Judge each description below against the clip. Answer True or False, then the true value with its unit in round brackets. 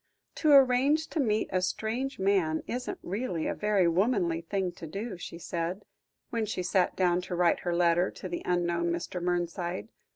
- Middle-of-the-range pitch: True (180 Hz)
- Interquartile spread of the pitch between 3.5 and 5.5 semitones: True (4.0 semitones)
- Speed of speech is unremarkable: True (175 wpm)